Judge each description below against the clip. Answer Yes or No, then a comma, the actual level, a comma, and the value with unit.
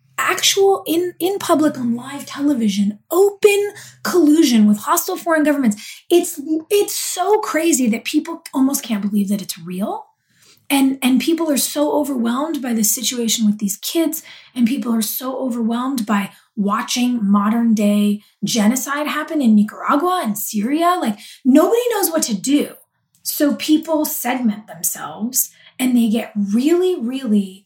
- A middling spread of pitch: No, wide, 6.4 semitones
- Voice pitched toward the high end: Yes, very high, 265 Hz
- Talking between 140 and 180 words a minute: Yes, average, 145 wpm